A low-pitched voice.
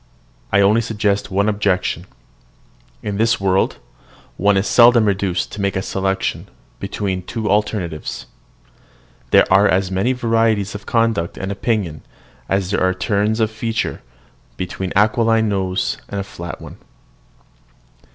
Yes: low, 100 Hz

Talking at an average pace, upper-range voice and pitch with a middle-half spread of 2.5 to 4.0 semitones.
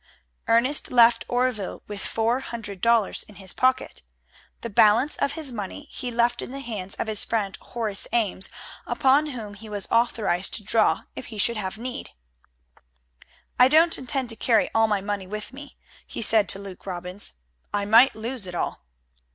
Yes: average, 175 wpm; high, 225 Hz; average, 3.3 semitones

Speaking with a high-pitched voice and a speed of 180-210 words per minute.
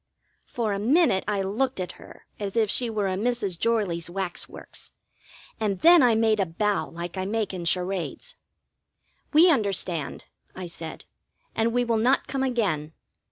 No: high, 205 Hz; average, 165 wpm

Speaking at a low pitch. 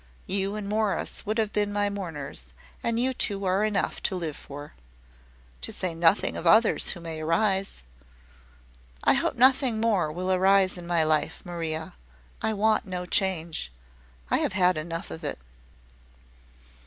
No: medium, 185 Hz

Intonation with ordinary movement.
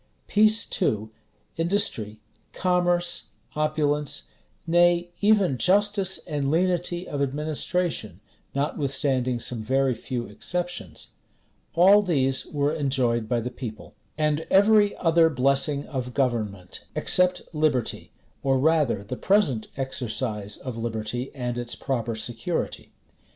No: wide, 6.3 semitones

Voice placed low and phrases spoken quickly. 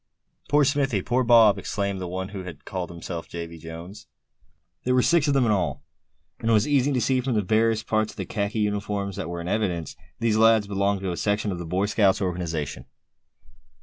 Yes: low, 100 Hz; fast, 215 wpm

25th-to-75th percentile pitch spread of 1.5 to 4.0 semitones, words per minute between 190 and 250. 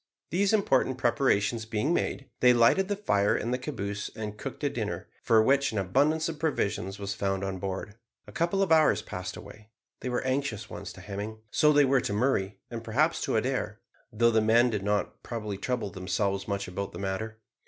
No: average, 5.0 semitones; average, 200 wpm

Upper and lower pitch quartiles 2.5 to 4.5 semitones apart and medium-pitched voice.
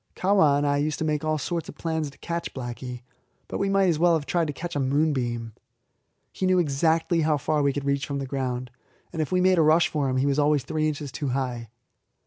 Yes: average, 3.1 semitones; medium, 150 Hz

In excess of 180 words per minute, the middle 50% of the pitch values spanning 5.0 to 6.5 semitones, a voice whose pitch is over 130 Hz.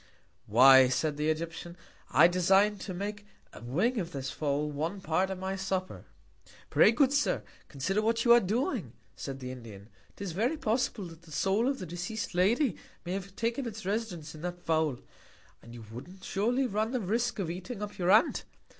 Yes: average, 190 wpm; wide, 5.6 semitones; medium, 185 Hz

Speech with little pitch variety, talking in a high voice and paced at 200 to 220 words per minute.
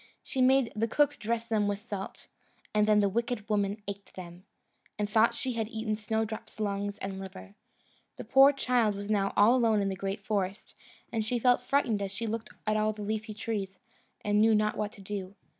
Yes: narrow, 2.1 semitones; high, 215 Hz; fast, 205 wpm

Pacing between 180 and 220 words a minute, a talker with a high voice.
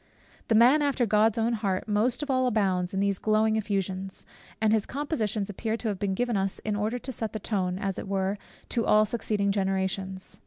Yes: fast, 205 wpm; high, 210 Hz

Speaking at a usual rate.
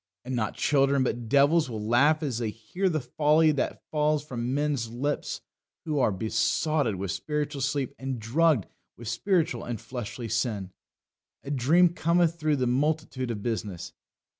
Yes: average, 160 wpm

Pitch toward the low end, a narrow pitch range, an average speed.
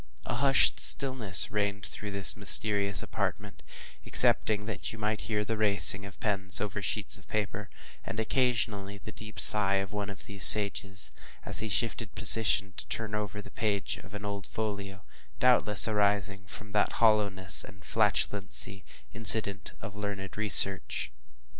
Yes: low, 105 Hz; narrow, 1.5 semitones; average, 155 wpm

